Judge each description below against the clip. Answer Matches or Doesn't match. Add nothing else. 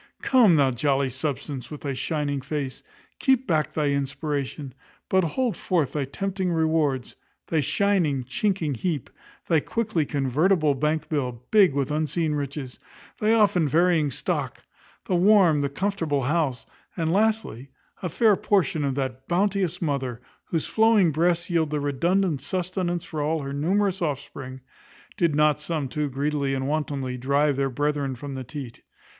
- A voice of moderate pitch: Matches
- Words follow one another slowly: Doesn't match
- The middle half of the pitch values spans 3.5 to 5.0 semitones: Matches